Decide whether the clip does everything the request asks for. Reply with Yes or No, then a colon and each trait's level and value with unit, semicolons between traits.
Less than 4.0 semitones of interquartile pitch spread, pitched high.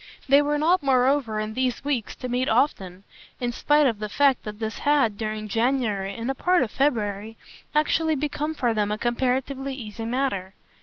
No: average, 4.6 semitones; very high, 250 Hz